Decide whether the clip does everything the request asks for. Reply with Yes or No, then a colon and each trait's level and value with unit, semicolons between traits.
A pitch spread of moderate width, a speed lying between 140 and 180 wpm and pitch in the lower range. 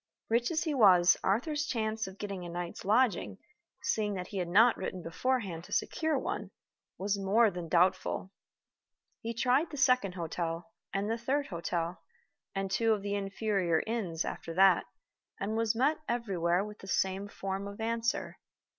No: average, 4.1 semitones; average, 165 wpm; high, 200 Hz